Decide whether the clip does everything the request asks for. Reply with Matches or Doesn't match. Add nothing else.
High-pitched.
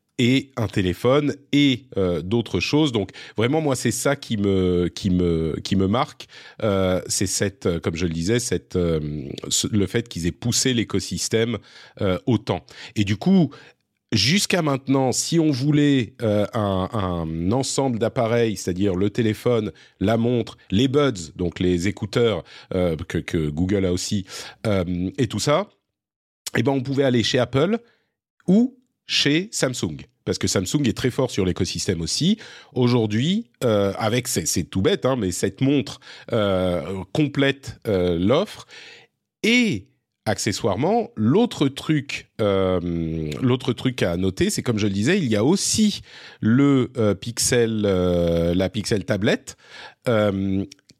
Doesn't match